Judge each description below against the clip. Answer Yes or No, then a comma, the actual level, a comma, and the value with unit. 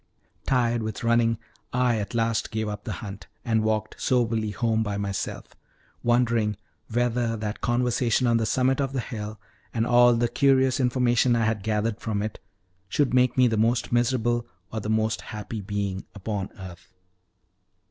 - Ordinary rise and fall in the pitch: No, narrow, 2.2 semitones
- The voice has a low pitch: Yes, low, 115 Hz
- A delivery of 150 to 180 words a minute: Yes, average, 165 wpm